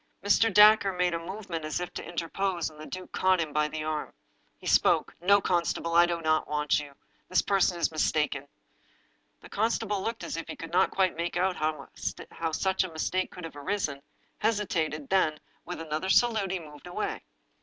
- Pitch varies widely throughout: No, average, 3.5 semitones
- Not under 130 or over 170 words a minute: No, average, 190 wpm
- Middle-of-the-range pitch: Yes, medium, 175 Hz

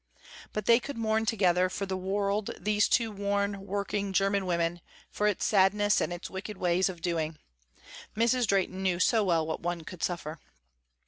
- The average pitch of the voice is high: Yes, high, 195 Hz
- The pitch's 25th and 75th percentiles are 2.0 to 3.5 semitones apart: Yes, average, 2.7 semitones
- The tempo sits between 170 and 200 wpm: Yes, average, 175 wpm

